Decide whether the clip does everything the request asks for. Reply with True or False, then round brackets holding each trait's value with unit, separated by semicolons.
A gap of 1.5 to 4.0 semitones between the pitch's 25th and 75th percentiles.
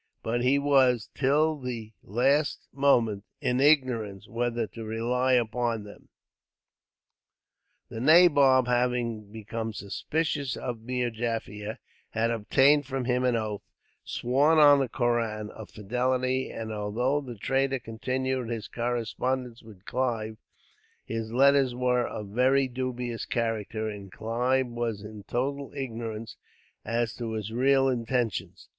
True (2.7 semitones)